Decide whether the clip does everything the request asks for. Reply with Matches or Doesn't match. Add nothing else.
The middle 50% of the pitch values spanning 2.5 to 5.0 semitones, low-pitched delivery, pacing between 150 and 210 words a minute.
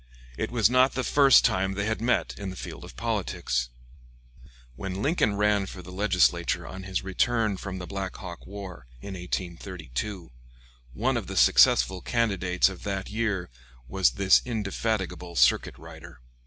Matches